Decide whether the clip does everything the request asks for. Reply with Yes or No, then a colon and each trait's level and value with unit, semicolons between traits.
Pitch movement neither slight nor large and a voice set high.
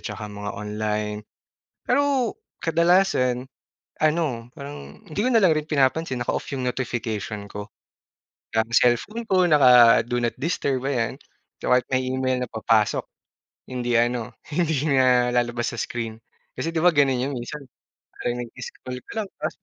No: average, 4.4 semitones; low, 125 Hz